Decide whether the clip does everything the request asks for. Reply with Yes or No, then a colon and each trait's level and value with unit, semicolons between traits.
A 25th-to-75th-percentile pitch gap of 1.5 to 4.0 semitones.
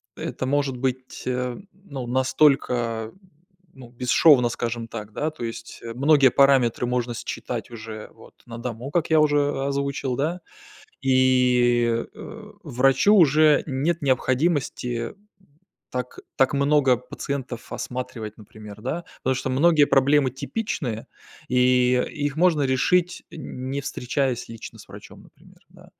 Yes: average, 3.0 semitones